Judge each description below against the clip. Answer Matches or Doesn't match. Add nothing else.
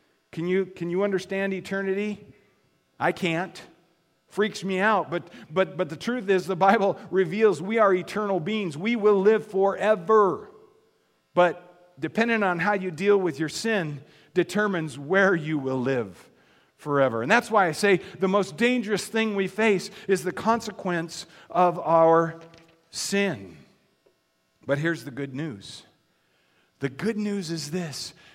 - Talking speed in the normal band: Matches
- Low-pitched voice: Doesn't match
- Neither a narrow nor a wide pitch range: Matches